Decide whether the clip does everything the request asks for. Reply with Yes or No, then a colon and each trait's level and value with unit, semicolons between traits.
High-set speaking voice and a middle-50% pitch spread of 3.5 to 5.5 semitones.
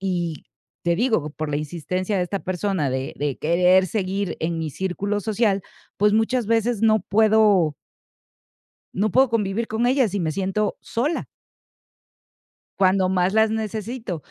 Yes: high, 195 Hz; average, 3.8 semitones